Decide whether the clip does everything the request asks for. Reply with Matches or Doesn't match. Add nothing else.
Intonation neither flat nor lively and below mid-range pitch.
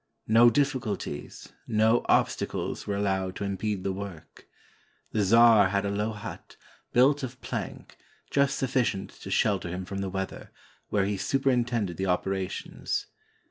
Matches